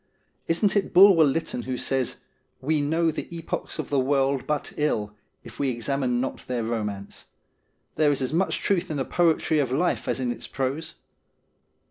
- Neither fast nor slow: Yes, average, 180 wpm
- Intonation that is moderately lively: Yes, average, 4.1 semitones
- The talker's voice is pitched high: No, medium, 140 Hz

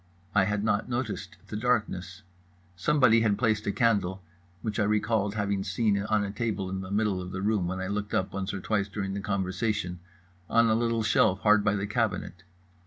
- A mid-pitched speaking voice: No, low, 105 Hz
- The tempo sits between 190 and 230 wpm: Yes, average, 200 wpm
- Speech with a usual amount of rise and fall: No, narrow, 2.3 semitones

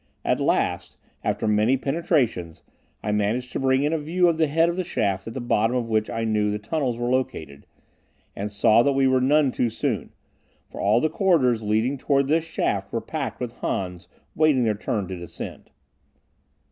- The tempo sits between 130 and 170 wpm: No, average, 195 wpm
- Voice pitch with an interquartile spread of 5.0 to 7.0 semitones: Yes, average, 5.3 semitones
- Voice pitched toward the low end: Yes, low, 125 Hz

